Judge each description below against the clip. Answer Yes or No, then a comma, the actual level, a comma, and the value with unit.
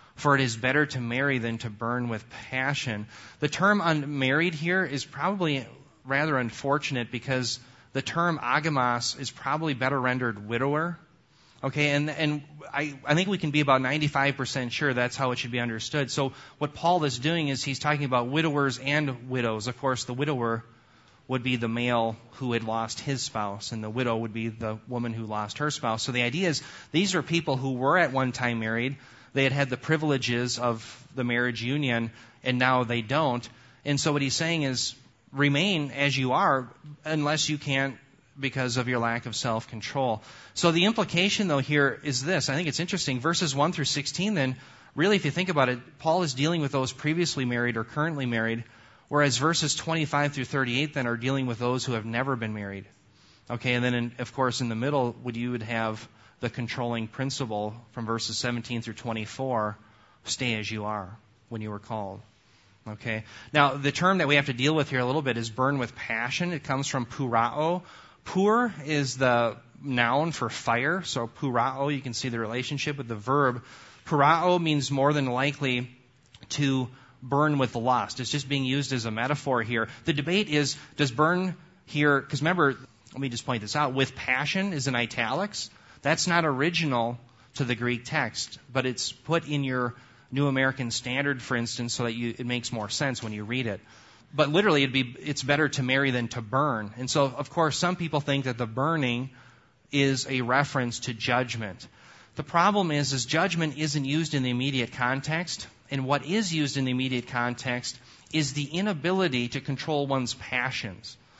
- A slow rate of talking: No, average, 190 wpm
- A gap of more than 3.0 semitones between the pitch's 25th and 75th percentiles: Yes, average, 3.5 semitones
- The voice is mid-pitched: No, low, 130 Hz